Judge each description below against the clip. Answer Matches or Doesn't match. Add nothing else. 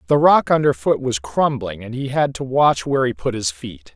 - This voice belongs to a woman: Doesn't match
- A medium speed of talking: Doesn't match